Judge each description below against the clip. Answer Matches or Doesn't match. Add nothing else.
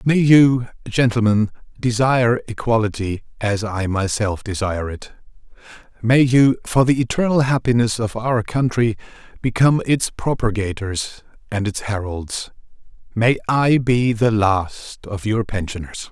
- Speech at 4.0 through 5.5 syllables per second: Matches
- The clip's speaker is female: Doesn't match